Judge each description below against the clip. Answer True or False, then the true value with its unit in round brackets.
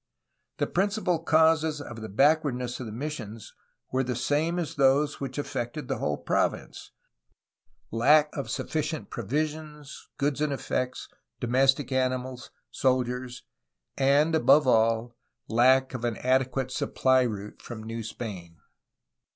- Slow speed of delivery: True (130 wpm)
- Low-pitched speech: True (130 Hz)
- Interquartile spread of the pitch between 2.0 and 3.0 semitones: False (3.8 semitones)